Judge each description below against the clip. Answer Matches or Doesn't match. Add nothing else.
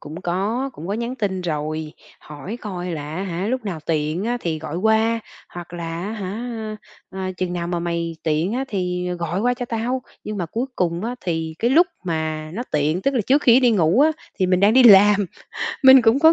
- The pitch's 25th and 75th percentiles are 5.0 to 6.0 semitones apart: Matches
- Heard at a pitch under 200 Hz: Matches